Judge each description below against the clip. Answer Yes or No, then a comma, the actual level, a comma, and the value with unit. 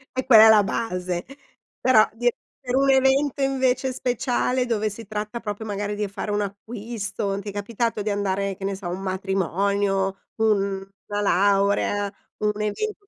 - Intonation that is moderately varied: Yes, average, 3.2 semitones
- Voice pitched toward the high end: Yes, high, 210 Hz